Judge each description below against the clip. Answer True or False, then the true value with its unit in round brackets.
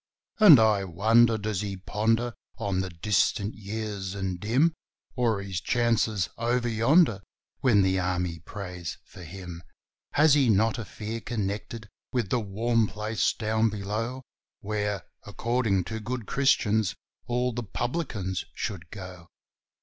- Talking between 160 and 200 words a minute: False (135 wpm)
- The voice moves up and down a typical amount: True (3.4 semitones)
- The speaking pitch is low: True (110 Hz)